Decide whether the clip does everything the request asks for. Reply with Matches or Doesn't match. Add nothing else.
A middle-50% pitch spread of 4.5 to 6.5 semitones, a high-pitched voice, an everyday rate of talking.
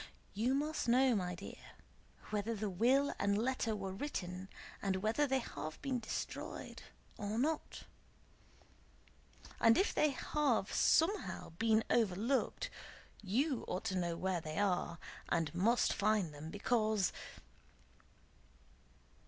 Doesn't match